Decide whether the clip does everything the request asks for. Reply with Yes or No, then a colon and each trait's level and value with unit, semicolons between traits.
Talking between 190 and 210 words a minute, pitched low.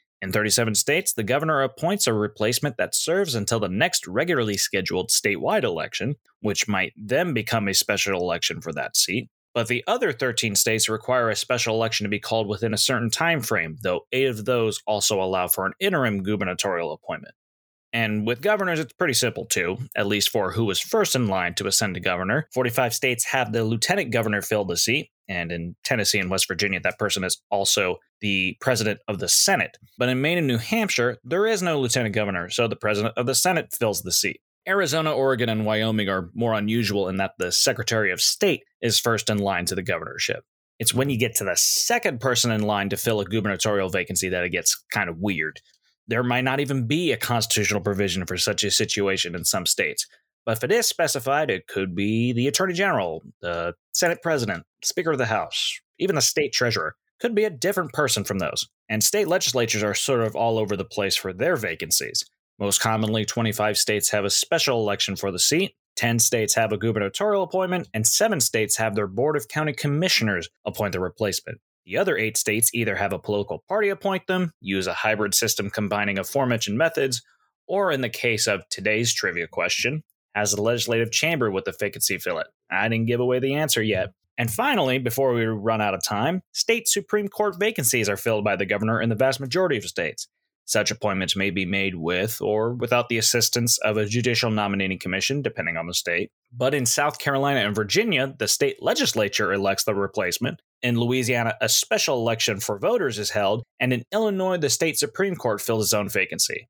Yes: fast, 205 wpm; low, 115 Hz